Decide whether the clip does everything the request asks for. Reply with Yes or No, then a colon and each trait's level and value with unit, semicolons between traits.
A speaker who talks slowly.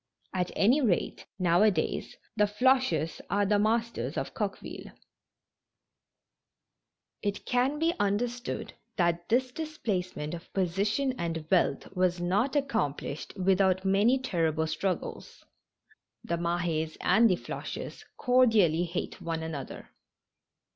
Yes: slow, 120 wpm